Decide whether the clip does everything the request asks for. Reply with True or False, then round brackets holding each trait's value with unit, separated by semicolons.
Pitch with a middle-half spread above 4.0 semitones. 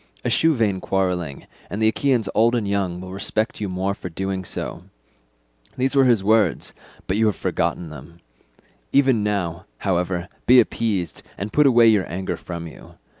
False (3.7 semitones)